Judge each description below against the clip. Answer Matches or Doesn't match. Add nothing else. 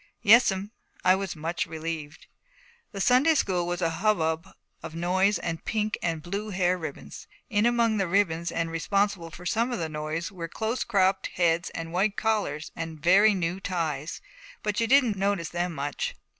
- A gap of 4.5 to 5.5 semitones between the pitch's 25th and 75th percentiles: Doesn't match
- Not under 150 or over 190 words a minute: Matches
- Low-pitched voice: Doesn't match